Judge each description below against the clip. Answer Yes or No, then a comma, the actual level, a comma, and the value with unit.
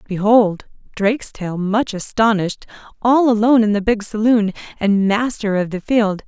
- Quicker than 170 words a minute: No, average, 145 wpm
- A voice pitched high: Yes, high, 215 Hz